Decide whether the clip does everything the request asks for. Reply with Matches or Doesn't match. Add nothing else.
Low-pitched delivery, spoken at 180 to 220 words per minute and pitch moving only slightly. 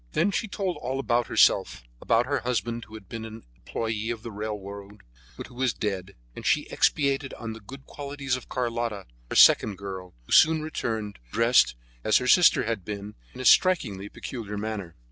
Doesn't match